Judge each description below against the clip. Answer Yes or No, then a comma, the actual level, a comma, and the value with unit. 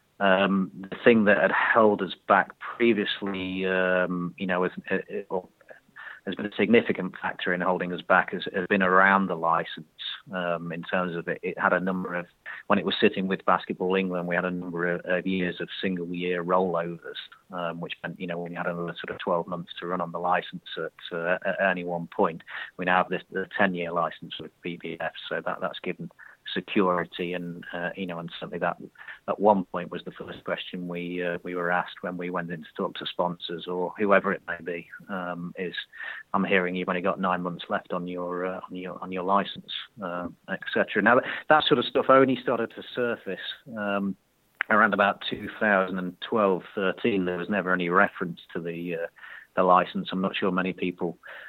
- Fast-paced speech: Yes, fast, 210 wpm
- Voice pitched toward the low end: Yes, very low, 90 Hz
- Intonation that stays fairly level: Yes, narrow, 1.3 semitones